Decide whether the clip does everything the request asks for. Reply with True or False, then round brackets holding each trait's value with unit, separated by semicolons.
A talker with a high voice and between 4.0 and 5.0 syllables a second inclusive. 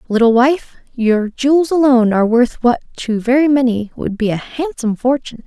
False (245 Hz; 5.4 syllables/s)